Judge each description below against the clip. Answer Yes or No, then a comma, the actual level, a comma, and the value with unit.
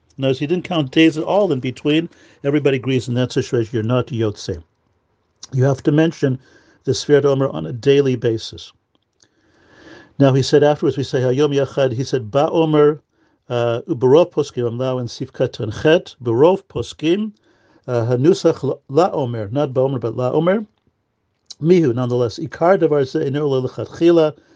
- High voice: No, low, 135 Hz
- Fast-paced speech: No, average, 150 wpm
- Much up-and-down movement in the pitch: No, average, 3.9 semitones